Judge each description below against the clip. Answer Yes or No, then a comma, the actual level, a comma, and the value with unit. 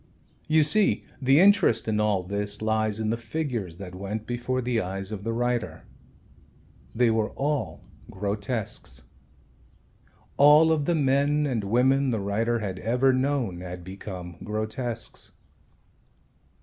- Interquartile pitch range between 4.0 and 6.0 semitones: Yes, average, 4.8 semitones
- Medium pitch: No, low, 115 Hz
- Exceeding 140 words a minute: No, slow, 135 wpm